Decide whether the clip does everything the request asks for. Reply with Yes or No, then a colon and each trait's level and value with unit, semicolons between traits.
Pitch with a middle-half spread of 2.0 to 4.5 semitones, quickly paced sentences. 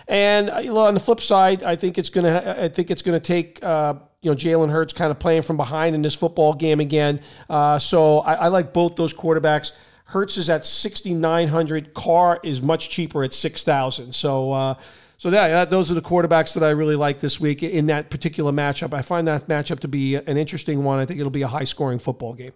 Yes: average, 2.7 semitones; fast, 210 wpm